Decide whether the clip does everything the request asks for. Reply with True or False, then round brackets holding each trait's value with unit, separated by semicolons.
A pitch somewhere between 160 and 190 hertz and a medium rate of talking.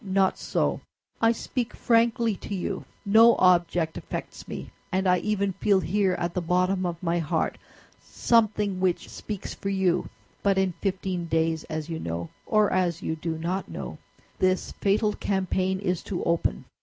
True (185 Hz; 165 wpm)